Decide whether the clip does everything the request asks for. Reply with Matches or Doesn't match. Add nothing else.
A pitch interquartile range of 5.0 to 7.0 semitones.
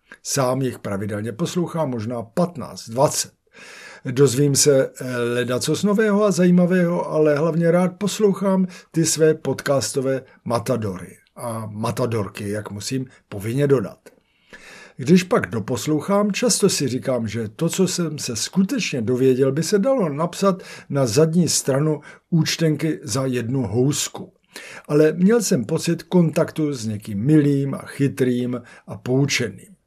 Matches